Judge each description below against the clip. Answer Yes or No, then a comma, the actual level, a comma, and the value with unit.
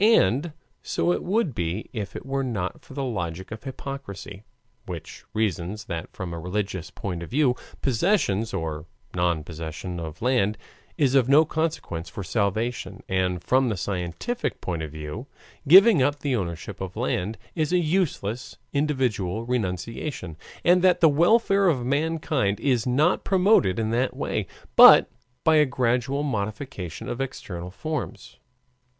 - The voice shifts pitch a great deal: Yes, wide, 7.7 semitones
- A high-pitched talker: No, low, 115 Hz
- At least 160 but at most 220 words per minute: No, average, 150 wpm